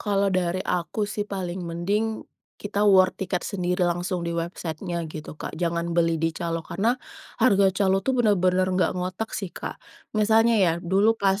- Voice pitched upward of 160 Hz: Yes, medium, 185 Hz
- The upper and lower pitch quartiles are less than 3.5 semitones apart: Yes, average, 2.9 semitones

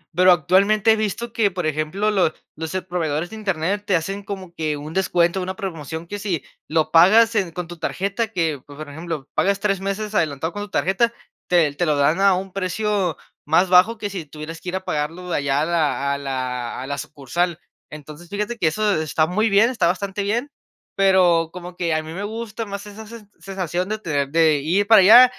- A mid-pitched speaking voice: Yes, medium, 180 Hz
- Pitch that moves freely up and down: No, average, 4.3 semitones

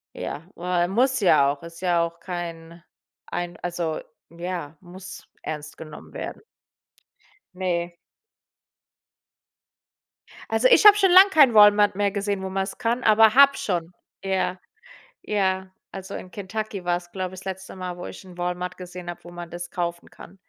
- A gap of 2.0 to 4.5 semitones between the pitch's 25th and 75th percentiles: Yes, narrow, 2.6 semitones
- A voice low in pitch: No, medium, 185 Hz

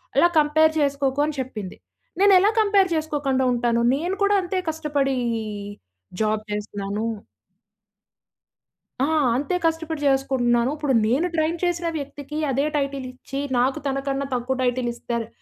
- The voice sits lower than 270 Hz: No, very high, 275 Hz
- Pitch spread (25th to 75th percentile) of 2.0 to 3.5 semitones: No, average, 3.9 semitones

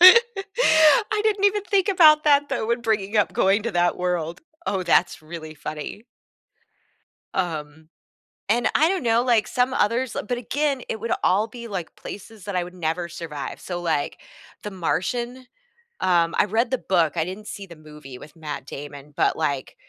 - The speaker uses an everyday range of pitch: No, wide, 7.2 semitones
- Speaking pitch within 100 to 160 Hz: No, high, 205 Hz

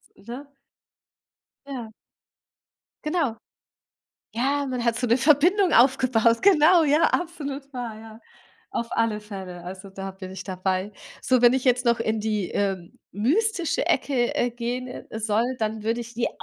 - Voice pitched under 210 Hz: No, high, 235 Hz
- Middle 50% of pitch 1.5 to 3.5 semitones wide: No, average, 4.3 semitones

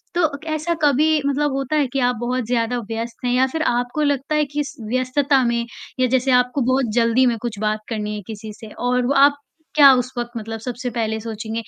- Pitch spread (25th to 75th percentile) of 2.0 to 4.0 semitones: Yes, average, 3.3 semitones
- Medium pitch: No, very high, 250 Hz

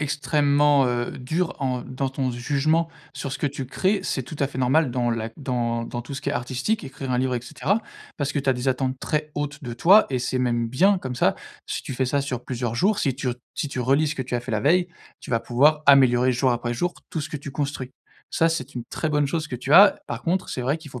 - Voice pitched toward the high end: No, low, 135 Hz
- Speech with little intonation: No, average, 3.2 semitones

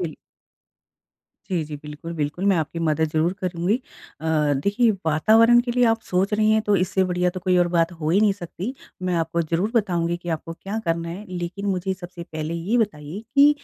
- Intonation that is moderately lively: Yes, average, 3.5 semitones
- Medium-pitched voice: Yes, medium, 180 Hz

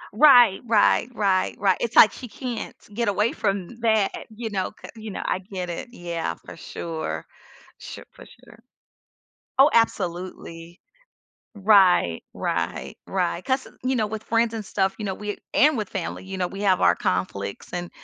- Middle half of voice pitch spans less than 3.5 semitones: No, average, 3.8 semitones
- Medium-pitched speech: No, high, 200 Hz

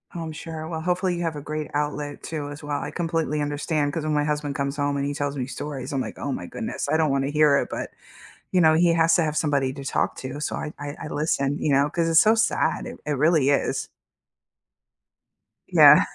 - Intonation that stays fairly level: Yes, narrow, 2.1 semitones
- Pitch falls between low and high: Yes, medium, 150 Hz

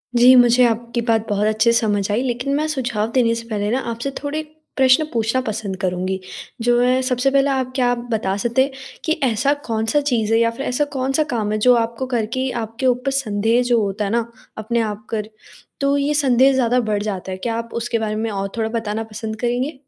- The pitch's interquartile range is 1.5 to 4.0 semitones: Yes, average, 2.9 semitones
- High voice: Yes, high, 235 Hz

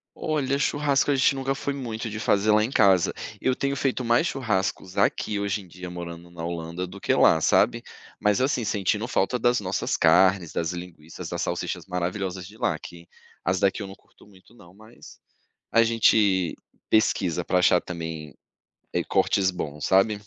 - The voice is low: Yes, low, 100 Hz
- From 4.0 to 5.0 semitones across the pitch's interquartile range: Yes, average, 4.4 semitones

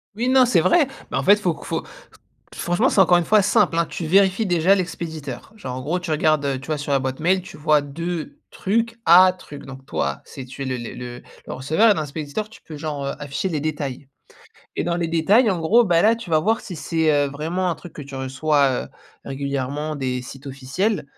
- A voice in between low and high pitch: Yes, medium, 160 Hz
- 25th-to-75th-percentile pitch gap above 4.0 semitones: Yes, average, 5.0 semitones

